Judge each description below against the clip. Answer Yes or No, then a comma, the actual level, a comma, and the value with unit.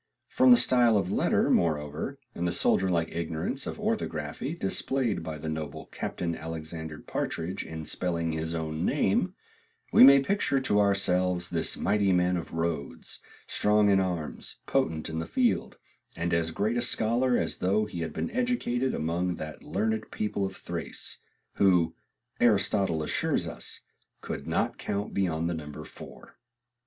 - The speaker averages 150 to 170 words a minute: Yes, average, 160 wpm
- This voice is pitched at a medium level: No, very low, 90 Hz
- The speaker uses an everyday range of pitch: Yes, average, 4.7 semitones